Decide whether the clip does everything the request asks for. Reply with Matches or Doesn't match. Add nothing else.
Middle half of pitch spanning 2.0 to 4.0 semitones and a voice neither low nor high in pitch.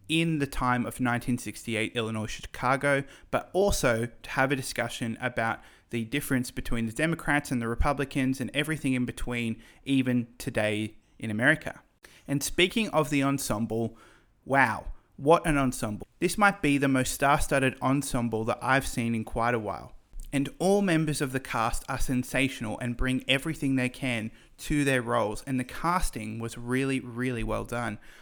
Doesn't match